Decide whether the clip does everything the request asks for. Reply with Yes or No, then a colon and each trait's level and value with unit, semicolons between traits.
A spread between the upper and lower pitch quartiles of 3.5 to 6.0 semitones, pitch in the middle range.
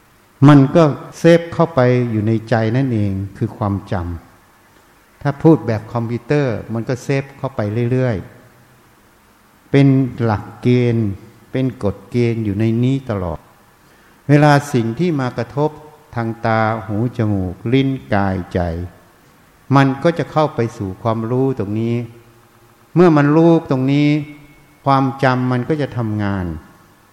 No: average, 4.3 semitones; low, 120 Hz